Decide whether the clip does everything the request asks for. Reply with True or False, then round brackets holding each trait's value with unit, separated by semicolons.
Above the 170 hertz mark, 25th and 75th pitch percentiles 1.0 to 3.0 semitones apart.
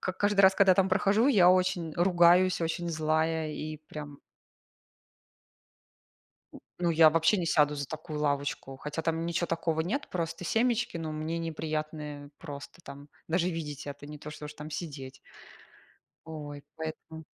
False (160 Hz; 2.6 semitones)